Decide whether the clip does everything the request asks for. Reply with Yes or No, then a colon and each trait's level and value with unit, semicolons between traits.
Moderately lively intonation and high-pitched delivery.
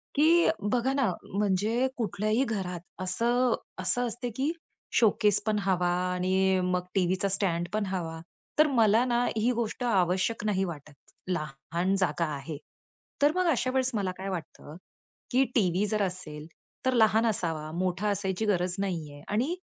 Yes: average, 4.5 semitones; high, 195 Hz